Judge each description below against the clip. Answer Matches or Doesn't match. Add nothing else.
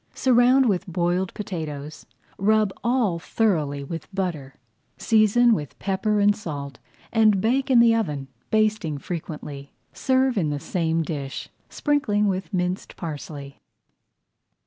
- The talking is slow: Matches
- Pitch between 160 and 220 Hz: Matches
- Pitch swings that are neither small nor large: Doesn't match